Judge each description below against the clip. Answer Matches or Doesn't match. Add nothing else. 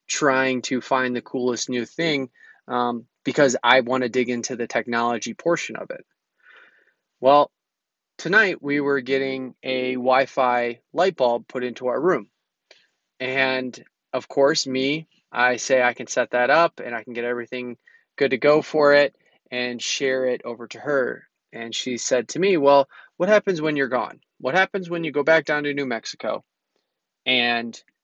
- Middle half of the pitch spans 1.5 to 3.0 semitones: Matches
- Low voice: Matches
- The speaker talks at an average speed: Matches